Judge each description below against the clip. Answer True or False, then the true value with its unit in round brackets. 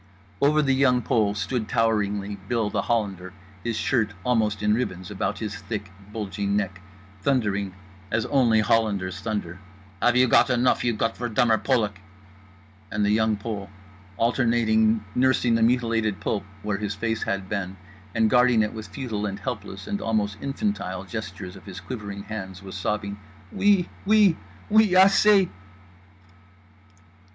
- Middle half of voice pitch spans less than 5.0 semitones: True (3.3 semitones)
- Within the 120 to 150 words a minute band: True (145 wpm)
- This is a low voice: True (110 Hz)